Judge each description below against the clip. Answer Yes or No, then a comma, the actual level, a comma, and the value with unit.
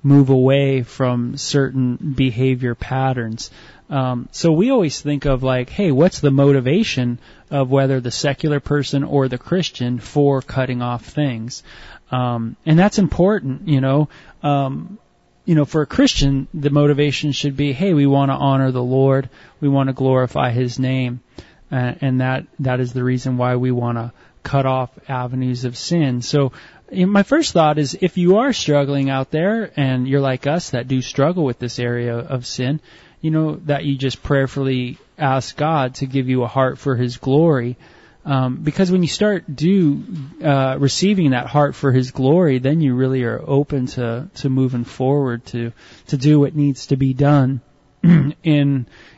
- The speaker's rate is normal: Yes, average, 175 wpm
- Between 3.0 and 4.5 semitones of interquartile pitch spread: No, narrow, 2.5 semitones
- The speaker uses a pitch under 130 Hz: No, low, 135 Hz